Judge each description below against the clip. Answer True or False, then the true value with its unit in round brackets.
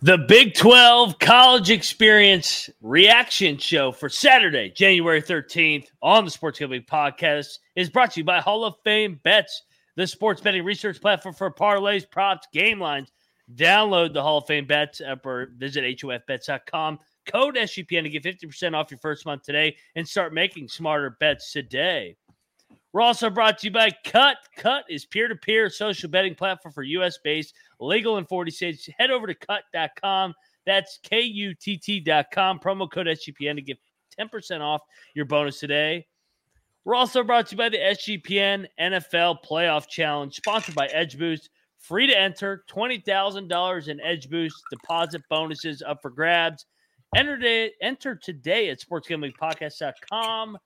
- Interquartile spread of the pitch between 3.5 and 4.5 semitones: False (5.3 semitones)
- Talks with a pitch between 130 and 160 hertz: False (180 Hz)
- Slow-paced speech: False (150 wpm)